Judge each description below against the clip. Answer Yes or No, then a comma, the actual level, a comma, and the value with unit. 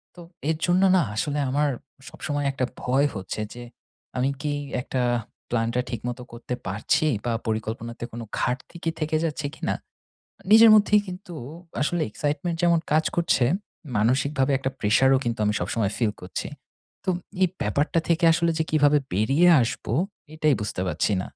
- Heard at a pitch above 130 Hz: Yes, medium, 140 Hz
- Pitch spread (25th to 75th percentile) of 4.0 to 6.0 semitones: Yes, average, 5.3 semitones